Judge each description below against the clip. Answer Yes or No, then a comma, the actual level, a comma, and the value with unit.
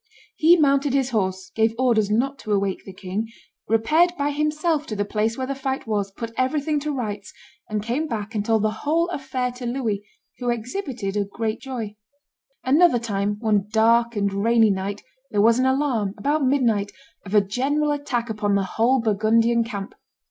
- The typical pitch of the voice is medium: No, high, 230 Hz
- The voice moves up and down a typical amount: Yes, average, 4.5 semitones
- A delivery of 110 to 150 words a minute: No, average, 180 wpm